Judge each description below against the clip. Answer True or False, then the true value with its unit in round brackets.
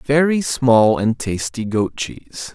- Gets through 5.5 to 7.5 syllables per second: False (3.7 syllables/s)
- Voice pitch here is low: True (120 Hz)